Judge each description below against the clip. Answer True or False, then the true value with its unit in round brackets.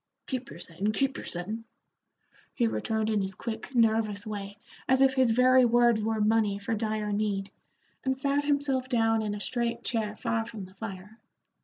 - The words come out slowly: False (180 wpm)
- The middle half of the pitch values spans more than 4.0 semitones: False (3.0 semitones)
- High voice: True (225 Hz)